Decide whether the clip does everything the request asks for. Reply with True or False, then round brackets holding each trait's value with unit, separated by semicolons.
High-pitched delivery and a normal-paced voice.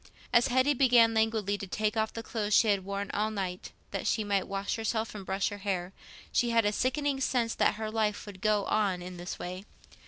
False (210 Hz; 225 wpm)